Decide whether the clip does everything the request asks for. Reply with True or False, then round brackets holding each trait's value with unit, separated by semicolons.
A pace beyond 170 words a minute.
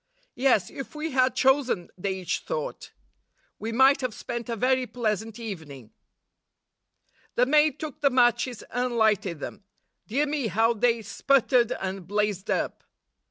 False (145 wpm)